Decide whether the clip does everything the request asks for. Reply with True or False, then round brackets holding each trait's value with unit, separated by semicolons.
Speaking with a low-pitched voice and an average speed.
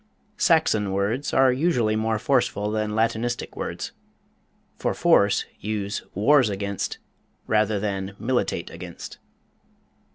False (110 Hz; 105 wpm)